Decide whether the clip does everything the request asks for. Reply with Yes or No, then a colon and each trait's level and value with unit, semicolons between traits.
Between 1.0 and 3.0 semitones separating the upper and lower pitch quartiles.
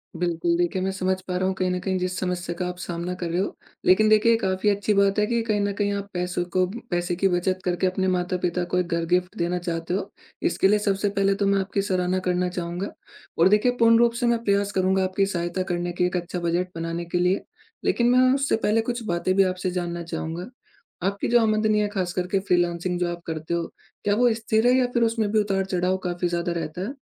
Yes: narrow, 2.4 semitones